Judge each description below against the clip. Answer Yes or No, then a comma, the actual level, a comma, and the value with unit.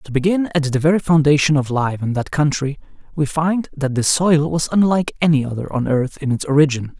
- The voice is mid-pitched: Yes, medium, 150 Hz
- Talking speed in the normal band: No, fast, 215 wpm